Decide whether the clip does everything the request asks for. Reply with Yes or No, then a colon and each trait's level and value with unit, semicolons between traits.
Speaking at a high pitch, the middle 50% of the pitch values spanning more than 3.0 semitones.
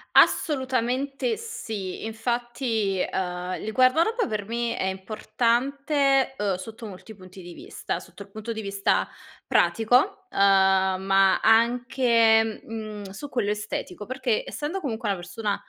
Yes: high, 225 Hz; average, 4.5 semitones